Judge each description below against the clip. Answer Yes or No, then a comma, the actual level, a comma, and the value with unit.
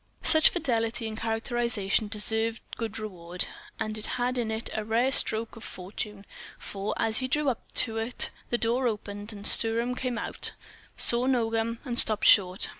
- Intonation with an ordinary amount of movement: No, narrow, 2.0 semitones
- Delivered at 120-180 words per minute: Yes, average, 165 wpm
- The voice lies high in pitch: Yes, high, 225 Hz